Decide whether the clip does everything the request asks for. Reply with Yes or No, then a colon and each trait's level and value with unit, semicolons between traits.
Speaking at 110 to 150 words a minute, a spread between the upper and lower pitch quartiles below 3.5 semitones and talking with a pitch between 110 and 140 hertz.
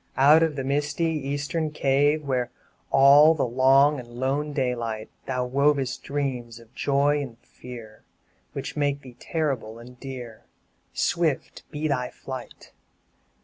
Yes: slow, 135 wpm; average, 2.7 semitones; low, 135 Hz